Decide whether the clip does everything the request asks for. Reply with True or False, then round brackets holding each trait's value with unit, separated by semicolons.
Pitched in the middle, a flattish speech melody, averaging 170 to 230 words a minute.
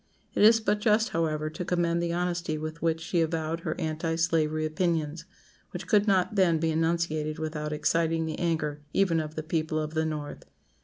True (165 Hz; 1.7 semitones; 190 wpm)